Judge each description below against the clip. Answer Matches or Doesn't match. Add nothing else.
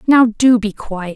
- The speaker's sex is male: Doesn't match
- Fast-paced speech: Matches